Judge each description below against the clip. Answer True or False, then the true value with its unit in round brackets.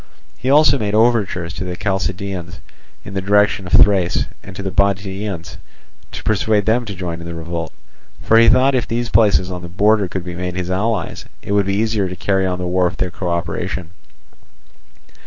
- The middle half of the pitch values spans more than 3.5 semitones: False (2.9 semitones)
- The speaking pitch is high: False (95 Hz)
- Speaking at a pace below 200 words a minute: False (205 wpm)